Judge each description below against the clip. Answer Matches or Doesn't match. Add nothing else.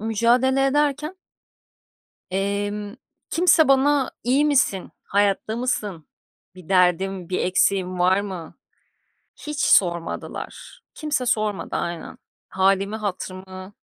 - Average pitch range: Doesn't match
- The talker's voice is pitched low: Doesn't match